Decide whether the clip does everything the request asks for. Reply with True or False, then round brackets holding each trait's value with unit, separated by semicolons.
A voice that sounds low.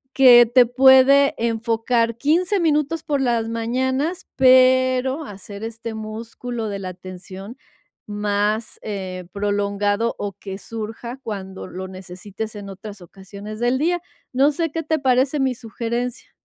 False (230 Hz)